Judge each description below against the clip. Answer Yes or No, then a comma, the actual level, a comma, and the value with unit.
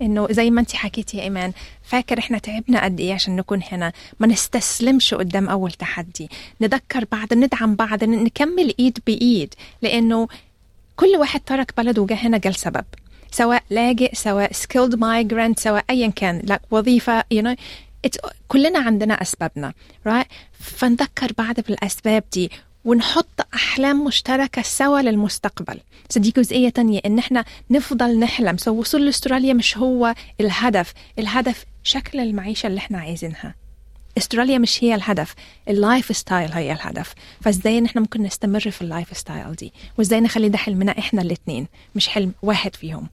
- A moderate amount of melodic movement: Yes, average, 3.4 semitones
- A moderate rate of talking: No, fast, 150 wpm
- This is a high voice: Yes, high, 225 Hz